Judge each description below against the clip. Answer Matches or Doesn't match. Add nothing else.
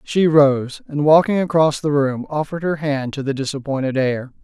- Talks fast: Doesn't match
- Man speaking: Matches